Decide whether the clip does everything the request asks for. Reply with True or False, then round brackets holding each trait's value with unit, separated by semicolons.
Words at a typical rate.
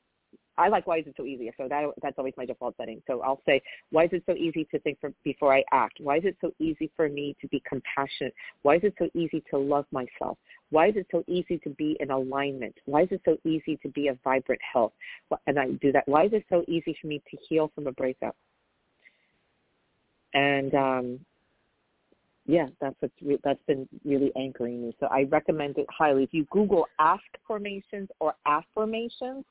False (210 wpm)